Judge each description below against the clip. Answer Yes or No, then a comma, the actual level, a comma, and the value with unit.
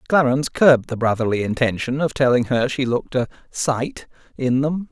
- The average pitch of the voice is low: Yes, low, 130 Hz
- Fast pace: No, average, 170 wpm